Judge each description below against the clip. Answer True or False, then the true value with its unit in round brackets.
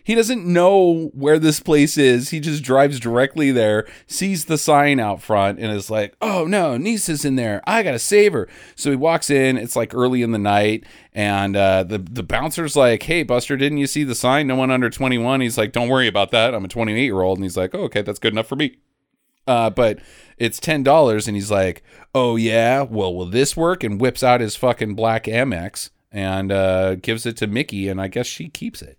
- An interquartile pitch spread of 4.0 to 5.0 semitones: False (5.5 semitones)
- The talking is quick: True (230 wpm)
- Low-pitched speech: True (125 Hz)